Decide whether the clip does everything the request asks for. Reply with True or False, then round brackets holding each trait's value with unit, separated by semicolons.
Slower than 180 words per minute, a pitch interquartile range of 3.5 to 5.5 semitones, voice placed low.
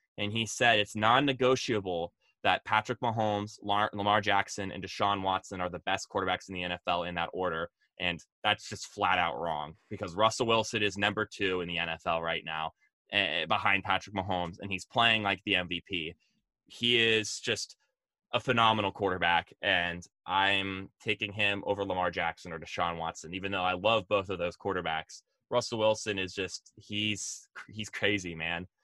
False (170 wpm; 3.0 semitones; 100 Hz)